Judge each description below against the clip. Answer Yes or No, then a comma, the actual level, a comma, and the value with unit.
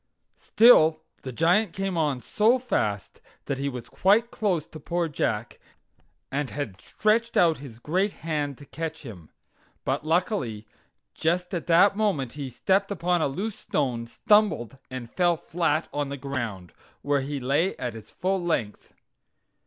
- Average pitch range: No, wide, 5.9 semitones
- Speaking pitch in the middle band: Yes, medium, 155 Hz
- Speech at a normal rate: Yes, average, 155 wpm